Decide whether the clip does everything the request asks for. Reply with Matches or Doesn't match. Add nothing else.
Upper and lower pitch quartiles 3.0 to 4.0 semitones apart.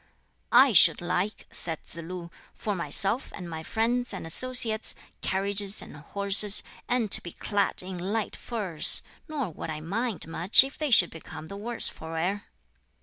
Doesn't match